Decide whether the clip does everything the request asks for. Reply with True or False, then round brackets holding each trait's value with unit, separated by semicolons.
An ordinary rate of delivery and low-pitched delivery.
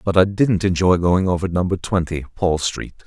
True (195 wpm; 90 Hz)